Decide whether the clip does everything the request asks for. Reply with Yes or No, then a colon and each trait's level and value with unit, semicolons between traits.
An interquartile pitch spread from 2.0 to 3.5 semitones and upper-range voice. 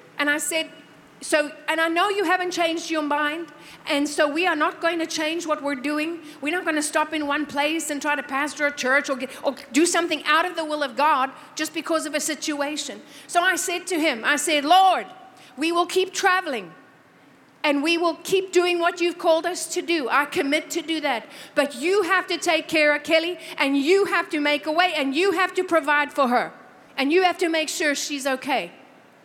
Yes: average, 2.8 semitones; very high, 315 Hz